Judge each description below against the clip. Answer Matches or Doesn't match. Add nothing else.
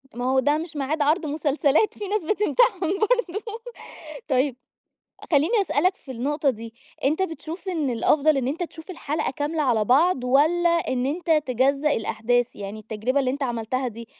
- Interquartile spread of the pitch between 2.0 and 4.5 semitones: Doesn't match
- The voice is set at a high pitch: Matches